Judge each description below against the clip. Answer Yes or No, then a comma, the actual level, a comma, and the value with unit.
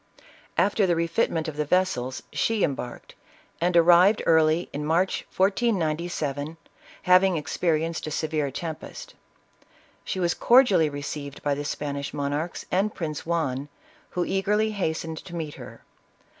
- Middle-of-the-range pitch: Yes, medium, 165 Hz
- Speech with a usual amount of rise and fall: Yes, average, 3.6 semitones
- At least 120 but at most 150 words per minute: Yes, average, 140 wpm